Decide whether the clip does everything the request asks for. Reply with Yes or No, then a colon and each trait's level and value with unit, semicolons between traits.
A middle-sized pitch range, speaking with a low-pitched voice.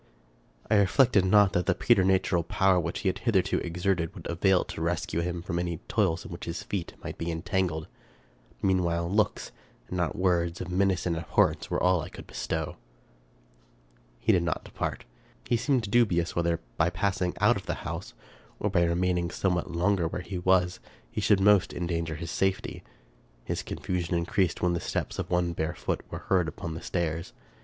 No: narrow, 2.1 semitones; very low, 90 Hz